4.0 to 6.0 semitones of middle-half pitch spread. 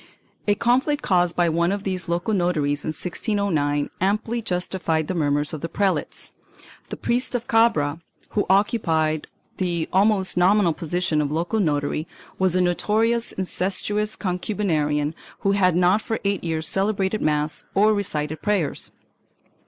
Yes: average, 4.5 semitones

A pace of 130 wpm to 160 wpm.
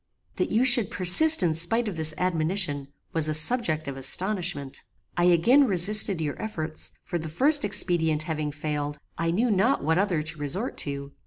No: average, 175 wpm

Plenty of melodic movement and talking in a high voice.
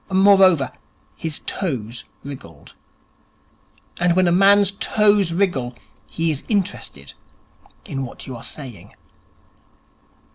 No: wide, 6.9 semitones; medium, 165 Hz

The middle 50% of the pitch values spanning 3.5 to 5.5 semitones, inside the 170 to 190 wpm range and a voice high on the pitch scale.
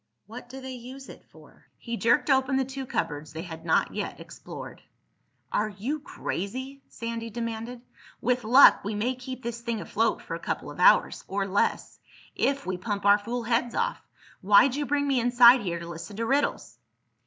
Yes: average, 4.1 semitones; average, 180 wpm; high, 235 Hz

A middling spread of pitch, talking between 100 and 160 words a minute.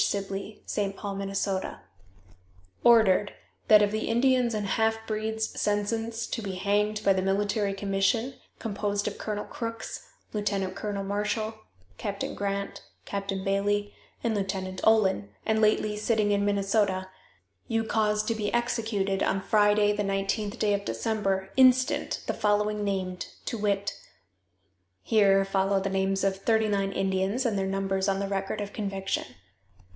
No: narrow, 1.7 semitones; average, 145 wpm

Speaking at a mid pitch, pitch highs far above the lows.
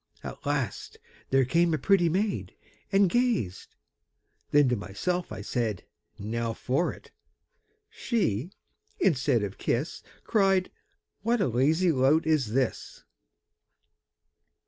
Yes: medium, 145 Hz; wide, 7.7 semitones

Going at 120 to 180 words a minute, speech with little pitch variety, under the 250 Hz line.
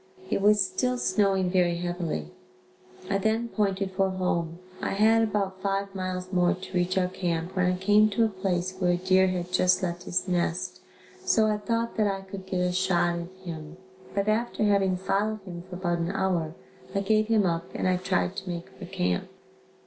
No: average, 200 wpm; narrow, 2.0 semitones; medium, 185 Hz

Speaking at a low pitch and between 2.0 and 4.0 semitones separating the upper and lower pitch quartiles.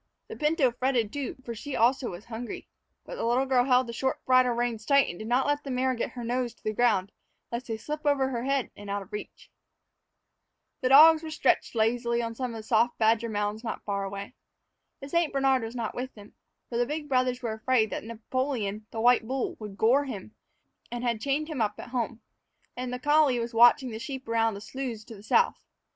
No: high, 240 Hz; average, 3.0 semitones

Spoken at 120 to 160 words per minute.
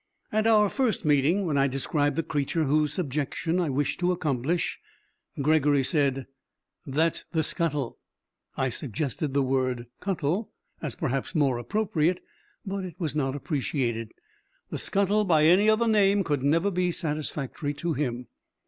Yes: average, 150 wpm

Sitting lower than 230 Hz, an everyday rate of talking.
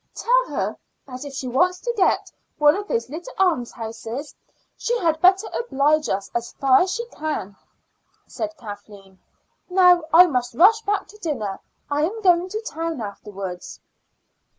No: very high, 310 Hz; average, 155 wpm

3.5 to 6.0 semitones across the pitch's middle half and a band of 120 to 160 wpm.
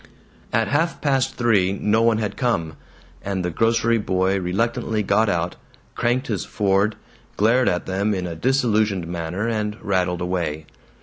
Yes: average, 4.1 semitones; average, 150 wpm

